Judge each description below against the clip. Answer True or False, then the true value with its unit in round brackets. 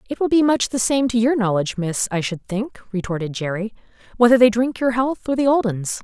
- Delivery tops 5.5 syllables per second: True (5.8 syllables/s)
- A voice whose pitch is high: True (230 Hz)